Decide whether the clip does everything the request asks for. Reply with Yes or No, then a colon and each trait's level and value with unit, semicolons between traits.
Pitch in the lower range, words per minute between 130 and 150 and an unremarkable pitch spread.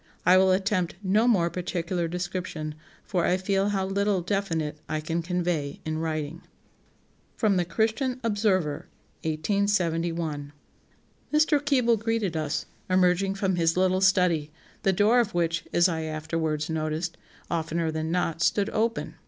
No: medium, 180 Hz; average, 140 wpm; average, 3.6 semitones